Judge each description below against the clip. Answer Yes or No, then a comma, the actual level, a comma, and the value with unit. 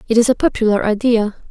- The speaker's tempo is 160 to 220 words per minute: Yes, average, 200 wpm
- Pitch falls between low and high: No, high, 225 Hz